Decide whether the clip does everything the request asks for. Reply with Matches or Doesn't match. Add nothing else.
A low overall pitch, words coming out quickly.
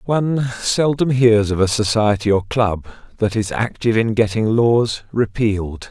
Doesn't match